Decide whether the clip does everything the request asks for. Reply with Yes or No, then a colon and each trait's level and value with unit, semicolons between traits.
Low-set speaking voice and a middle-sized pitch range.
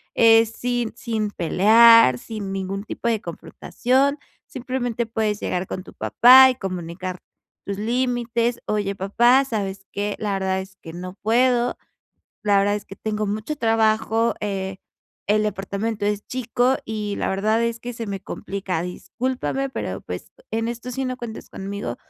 No: high, 220 Hz; average, 3.3 semitones